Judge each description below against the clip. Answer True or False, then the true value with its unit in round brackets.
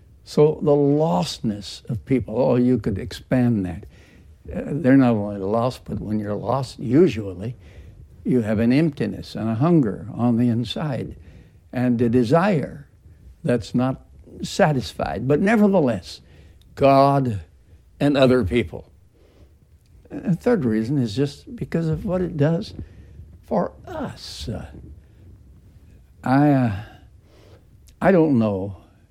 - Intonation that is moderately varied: False (6.6 semitones)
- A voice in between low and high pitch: False (115 Hz)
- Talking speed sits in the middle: False (125 wpm)